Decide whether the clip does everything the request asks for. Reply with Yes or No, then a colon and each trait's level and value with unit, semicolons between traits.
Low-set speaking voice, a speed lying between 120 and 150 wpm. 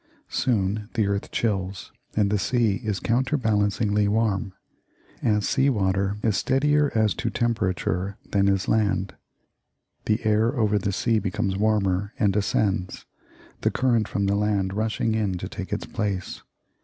Yes: low, 105 Hz; average, 145 wpm